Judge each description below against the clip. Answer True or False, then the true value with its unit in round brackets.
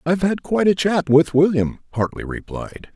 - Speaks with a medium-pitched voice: True (165 Hz)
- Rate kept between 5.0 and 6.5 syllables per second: True (5.4 syllables/s)